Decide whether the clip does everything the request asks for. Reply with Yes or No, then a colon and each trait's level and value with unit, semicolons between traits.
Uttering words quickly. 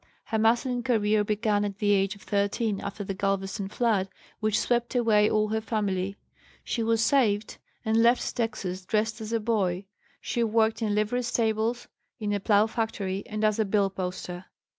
No: average, 175 wpm